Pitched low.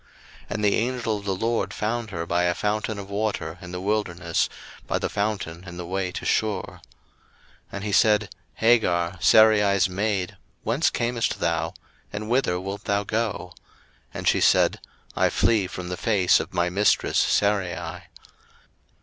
Yes: low, 100 Hz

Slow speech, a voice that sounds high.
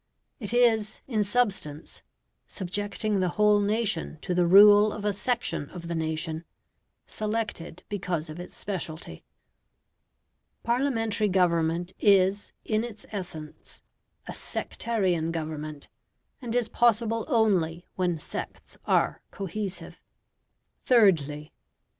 Yes: slow, 110 wpm; high, 195 Hz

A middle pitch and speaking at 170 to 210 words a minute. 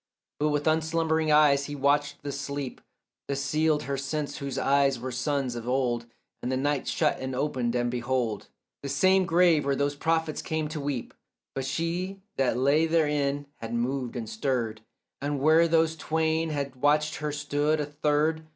Yes: medium, 145 Hz; average, 175 wpm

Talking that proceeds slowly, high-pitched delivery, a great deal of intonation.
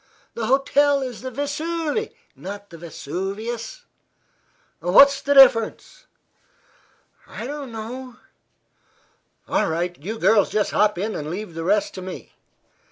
Yes: slow, 125 wpm; high, 225 Hz; wide, 6.1 semitones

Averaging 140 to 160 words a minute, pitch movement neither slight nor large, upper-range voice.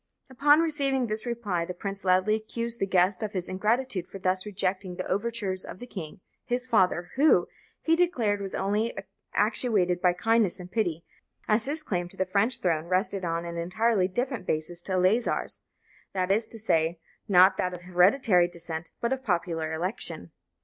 No: average, 175 wpm; average, 4.3 semitones; high, 195 Hz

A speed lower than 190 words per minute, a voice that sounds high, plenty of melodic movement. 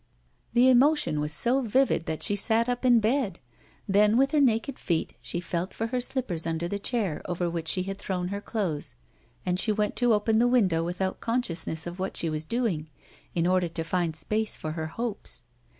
No: fast, 205 wpm; high, 200 Hz; wide, 5.8 semitones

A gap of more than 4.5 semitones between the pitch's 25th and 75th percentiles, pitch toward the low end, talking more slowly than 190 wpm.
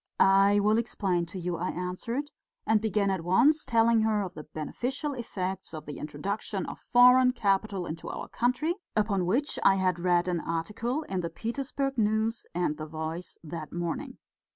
No: average, 5.0 semitones; high, 195 Hz; average, 175 wpm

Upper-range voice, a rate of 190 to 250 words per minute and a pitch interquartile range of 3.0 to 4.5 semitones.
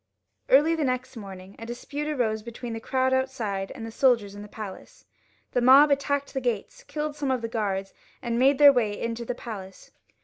Yes: high, 240 Hz; average, 200 wpm; average, 3.7 semitones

